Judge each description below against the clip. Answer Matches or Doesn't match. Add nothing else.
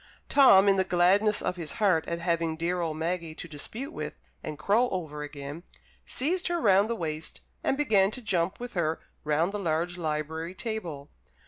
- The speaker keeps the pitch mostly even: Doesn't match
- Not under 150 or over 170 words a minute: Doesn't match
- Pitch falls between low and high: Matches